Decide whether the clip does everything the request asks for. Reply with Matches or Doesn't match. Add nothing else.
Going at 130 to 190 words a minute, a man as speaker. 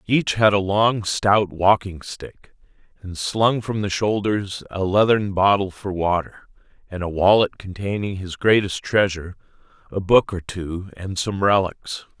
Matches